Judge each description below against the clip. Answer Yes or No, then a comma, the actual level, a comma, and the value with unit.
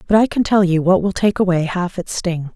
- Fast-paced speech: Yes, fast, 280 wpm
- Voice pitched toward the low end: No, medium, 185 Hz